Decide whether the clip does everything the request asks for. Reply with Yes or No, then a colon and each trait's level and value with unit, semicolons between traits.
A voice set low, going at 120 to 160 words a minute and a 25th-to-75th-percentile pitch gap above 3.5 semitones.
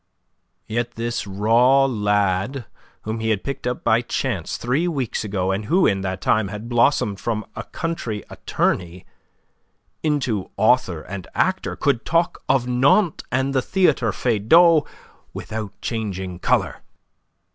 Yes: low, 115 Hz; slow, 135 wpm; average, 4.7 semitones